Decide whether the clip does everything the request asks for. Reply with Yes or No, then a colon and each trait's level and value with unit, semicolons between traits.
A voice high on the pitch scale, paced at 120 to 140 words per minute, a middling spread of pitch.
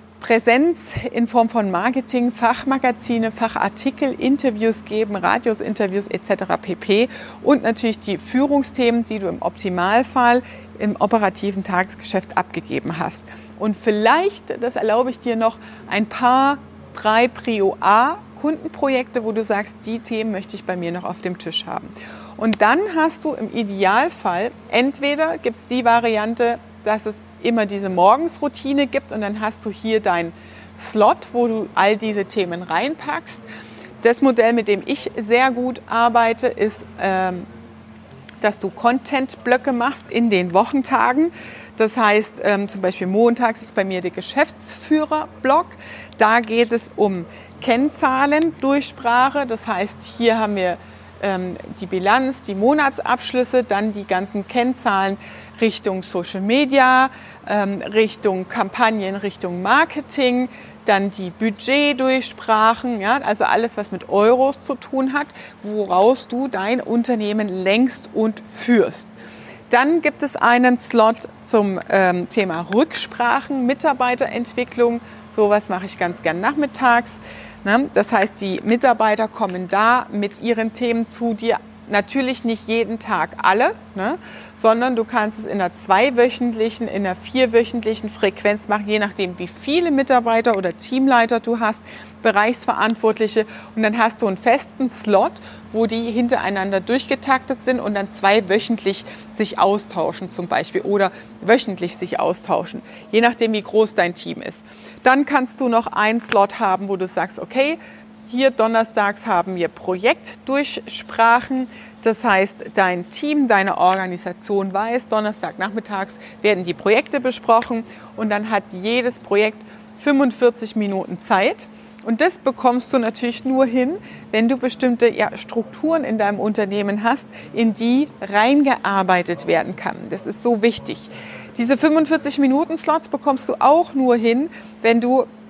Yes: high, 225 Hz; average, 135 wpm; average, 3.7 semitones